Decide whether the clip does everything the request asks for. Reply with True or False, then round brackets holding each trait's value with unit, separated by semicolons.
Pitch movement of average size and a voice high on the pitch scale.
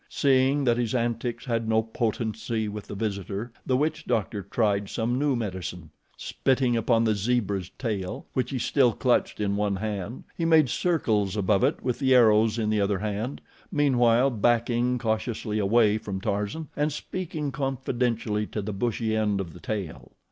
False (3.3 semitones; 115 Hz)